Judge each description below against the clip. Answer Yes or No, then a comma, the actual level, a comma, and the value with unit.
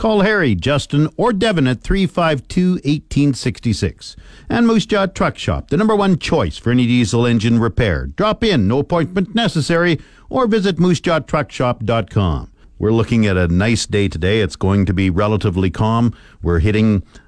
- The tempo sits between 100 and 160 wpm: Yes, average, 155 wpm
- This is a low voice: Yes, low, 120 Hz